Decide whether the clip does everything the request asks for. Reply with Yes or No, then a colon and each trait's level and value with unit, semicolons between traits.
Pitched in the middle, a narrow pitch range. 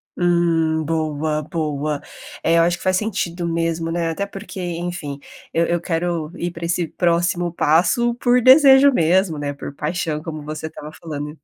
Yes: medium, 170 Hz; narrow, 2.1 semitones